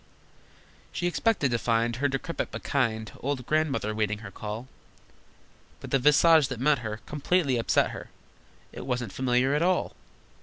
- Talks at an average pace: Yes, average, 155 wpm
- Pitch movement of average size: Yes, average, 4.6 semitones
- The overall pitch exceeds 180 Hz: No, low, 130 Hz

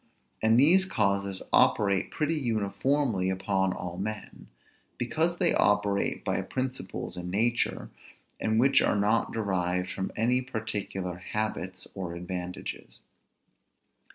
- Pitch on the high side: No, low, 105 Hz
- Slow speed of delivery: Yes, slow, 115 wpm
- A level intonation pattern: No, average, 4.2 semitones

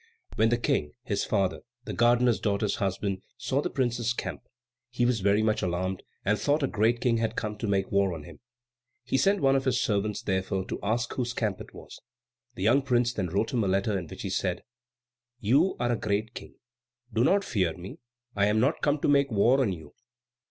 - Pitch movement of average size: Yes, average, 4.0 semitones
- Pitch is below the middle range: Yes, low, 110 Hz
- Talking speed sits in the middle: No, fast, 215 wpm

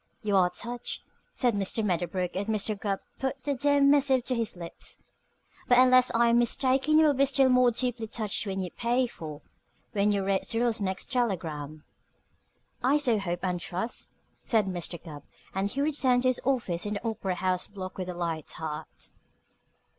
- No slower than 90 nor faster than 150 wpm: No, average, 185 wpm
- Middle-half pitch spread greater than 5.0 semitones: Yes, wide, 5.5 semitones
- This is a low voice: No, high, 215 Hz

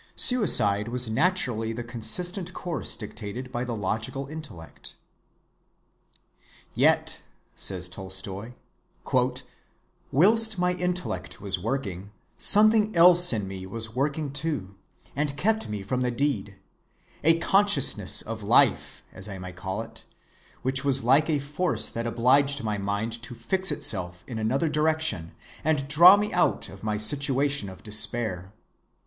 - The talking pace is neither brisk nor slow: No, slow, 130 wpm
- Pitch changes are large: Yes, wide, 7.2 semitones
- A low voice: Yes, low, 125 Hz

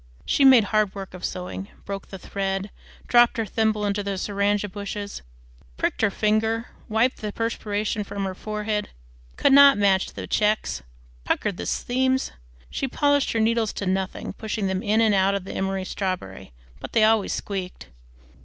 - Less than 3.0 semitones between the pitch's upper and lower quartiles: Yes, narrow, 2.4 semitones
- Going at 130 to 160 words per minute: No, average, 170 wpm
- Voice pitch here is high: Yes, high, 205 Hz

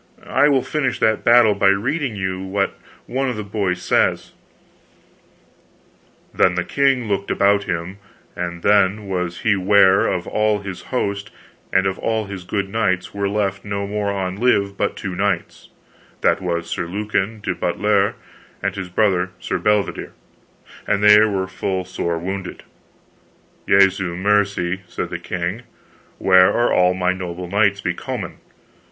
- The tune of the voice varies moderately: No, narrow, 2.1 semitones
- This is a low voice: Yes, low, 100 Hz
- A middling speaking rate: Yes, average, 150 wpm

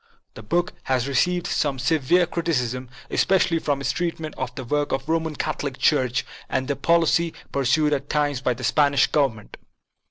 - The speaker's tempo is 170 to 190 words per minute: Yes, average, 180 wpm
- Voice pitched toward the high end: No, medium, 145 Hz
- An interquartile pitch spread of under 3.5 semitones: No, average, 3.8 semitones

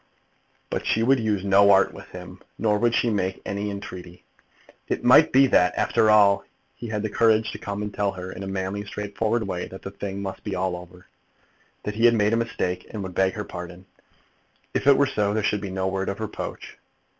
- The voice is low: Yes, low, 100 Hz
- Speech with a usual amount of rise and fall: No, narrow, 2.3 semitones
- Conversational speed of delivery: No, fast, 220 wpm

